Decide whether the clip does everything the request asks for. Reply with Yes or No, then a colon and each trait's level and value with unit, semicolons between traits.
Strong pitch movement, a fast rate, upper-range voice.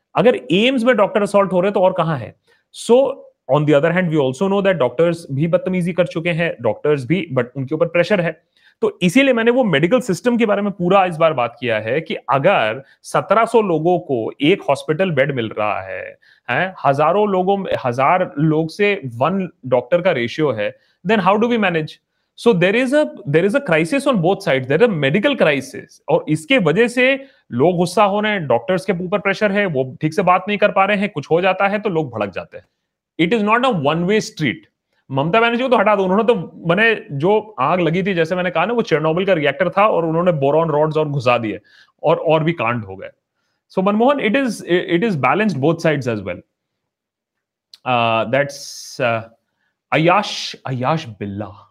No: wide, 5.7 semitones; fast, 195 wpm; medium, 180 Hz